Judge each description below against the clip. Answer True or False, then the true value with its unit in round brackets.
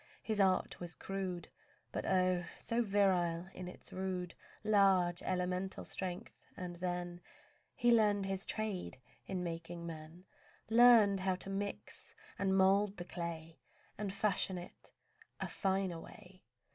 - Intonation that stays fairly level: True (2.0 semitones)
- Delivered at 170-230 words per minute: False (135 wpm)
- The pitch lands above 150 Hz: True (185 Hz)